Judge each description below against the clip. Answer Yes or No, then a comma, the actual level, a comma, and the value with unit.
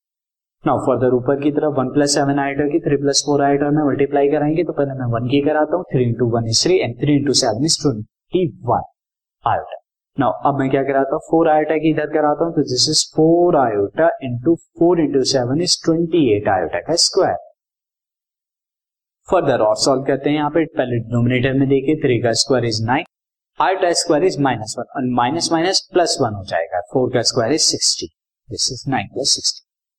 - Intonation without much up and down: No, average, 3.6 semitones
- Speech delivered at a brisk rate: No, average, 145 wpm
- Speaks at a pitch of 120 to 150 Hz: Yes, medium, 140 Hz